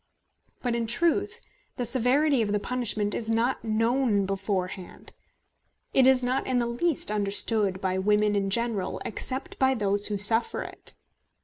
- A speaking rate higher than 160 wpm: No, average, 150 wpm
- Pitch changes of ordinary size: Yes, average, 3.6 semitones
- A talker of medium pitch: No, high, 225 Hz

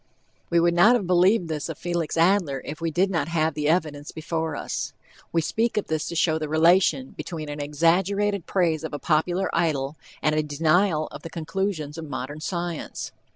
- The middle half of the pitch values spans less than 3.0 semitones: Yes, narrow, 2.6 semitones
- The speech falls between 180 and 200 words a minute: Yes, average, 195 wpm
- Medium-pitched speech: Yes, medium, 165 Hz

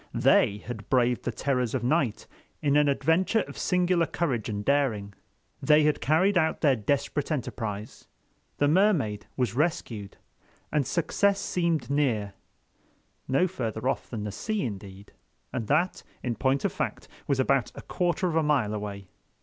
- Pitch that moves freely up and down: Yes, wide, 6.5 semitones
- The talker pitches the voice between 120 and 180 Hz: Yes, low, 135 Hz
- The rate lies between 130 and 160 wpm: Yes, average, 155 wpm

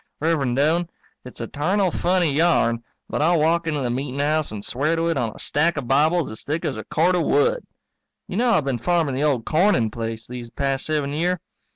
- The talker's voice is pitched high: No, medium, 150 Hz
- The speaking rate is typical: No, fast, 215 wpm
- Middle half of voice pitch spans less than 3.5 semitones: No, average, 4.9 semitones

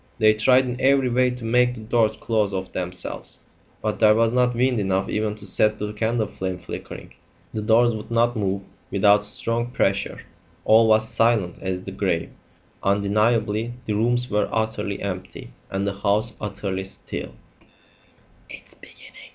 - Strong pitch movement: No, average, 2.7 semitones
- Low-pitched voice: Yes, low, 110 Hz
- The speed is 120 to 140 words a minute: No, average, 155 wpm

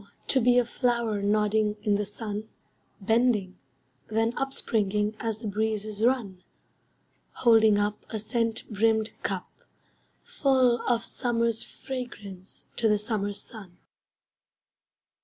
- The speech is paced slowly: Yes, slow, 115 wpm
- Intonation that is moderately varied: No, narrow, 2.2 semitones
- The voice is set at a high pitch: Yes, high, 220 Hz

